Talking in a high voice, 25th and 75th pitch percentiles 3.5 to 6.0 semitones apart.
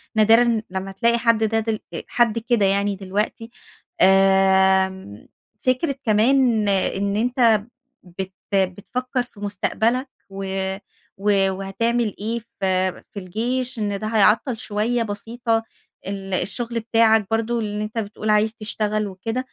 No: high, 215 Hz; average, 3.0 semitones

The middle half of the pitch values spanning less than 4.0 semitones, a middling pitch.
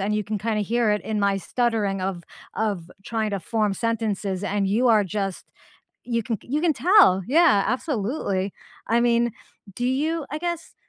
No: average, 3.5 semitones; high, 220 Hz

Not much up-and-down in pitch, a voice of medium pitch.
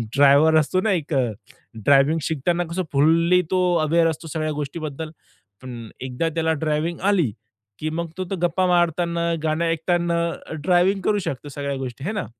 No: average, 3.0 semitones; medium, 160 Hz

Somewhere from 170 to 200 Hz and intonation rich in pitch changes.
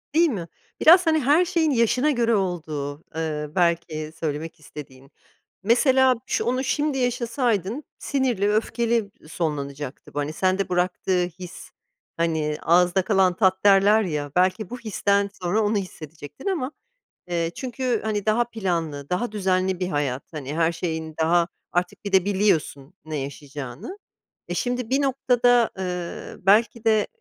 Yes: high, 190 Hz; wide, 6.5 semitones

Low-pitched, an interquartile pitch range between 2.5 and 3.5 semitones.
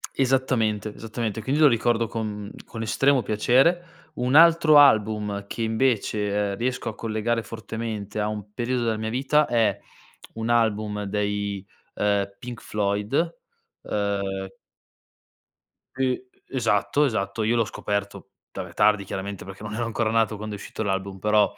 Yes: low, 110 Hz; average, 2.8 semitones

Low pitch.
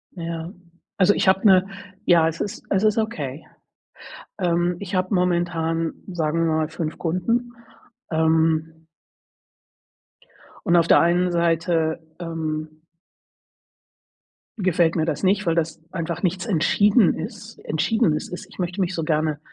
No: medium, 170 Hz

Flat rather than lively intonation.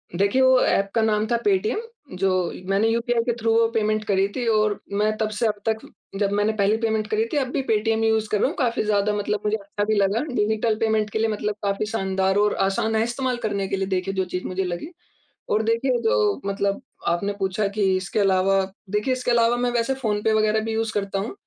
Yes: narrow, 2.2 semitones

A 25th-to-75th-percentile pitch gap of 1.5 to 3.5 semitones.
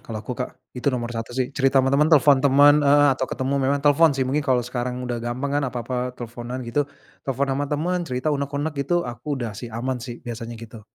Yes: average, 2.8 semitones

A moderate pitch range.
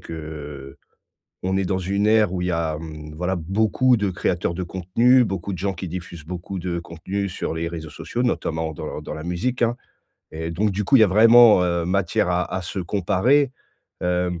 Yes: average, 3.6 semitones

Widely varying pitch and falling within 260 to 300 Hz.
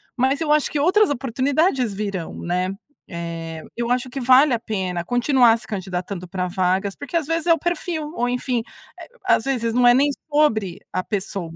No: wide, 7.2 semitones; high, 240 Hz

